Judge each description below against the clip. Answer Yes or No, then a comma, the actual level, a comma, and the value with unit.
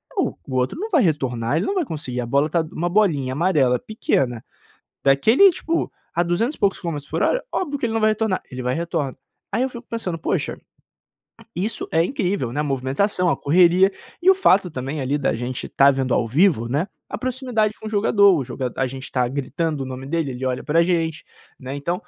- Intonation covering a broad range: Yes, wide, 7.6 semitones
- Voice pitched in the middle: Yes, medium, 160 Hz